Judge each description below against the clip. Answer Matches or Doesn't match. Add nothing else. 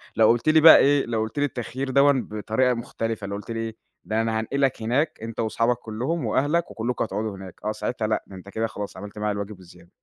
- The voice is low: Matches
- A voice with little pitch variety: Doesn't match